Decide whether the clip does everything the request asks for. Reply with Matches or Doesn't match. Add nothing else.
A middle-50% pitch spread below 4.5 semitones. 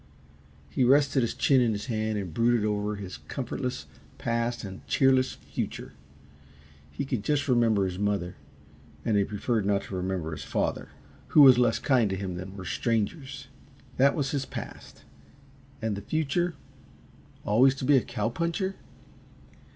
Doesn't match